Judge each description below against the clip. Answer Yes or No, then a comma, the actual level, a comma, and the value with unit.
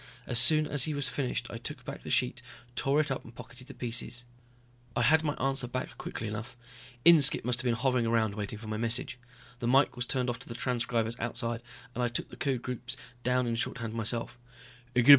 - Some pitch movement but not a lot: No, narrow, 2.2 semitones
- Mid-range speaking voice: No, low, 120 Hz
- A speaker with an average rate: No, fast, 215 wpm